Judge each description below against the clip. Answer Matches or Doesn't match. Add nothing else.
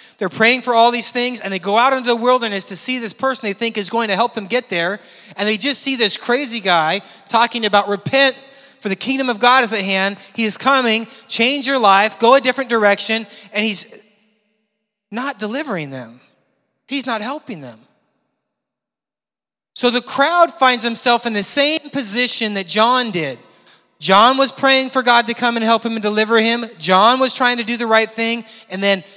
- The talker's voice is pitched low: Doesn't match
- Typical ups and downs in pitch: Matches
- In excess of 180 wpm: Matches